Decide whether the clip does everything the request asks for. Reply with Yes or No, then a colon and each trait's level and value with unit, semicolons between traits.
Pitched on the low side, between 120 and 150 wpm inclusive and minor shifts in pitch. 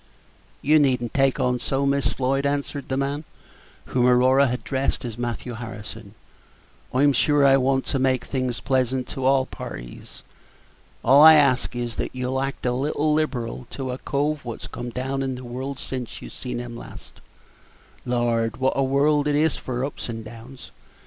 No: low, 130 Hz; average, 180 wpm; narrow, 2.2 semitones